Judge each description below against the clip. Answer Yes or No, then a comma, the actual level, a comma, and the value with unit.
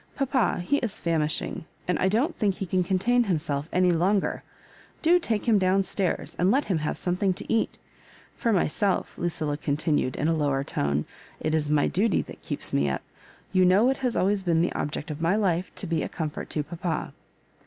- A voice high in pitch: No, medium, 180 Hz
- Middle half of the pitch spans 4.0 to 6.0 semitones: Yes, average, 4.7 semitones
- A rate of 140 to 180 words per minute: No, fast, 205 wpm